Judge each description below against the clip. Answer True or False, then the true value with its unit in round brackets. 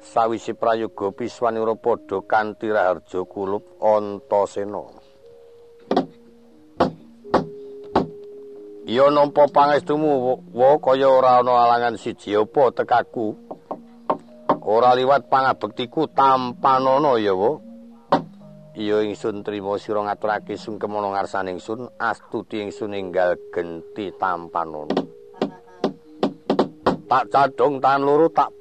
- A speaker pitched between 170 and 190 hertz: False (125 Hz)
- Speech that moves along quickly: False (85 wpm)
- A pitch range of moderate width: False (6.8 semitones)